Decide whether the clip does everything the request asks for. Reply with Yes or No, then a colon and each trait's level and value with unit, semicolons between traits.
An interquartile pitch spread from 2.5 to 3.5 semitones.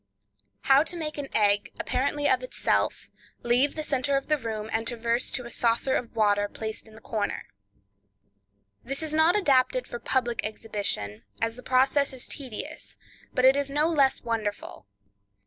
No: average, 4.6 semitones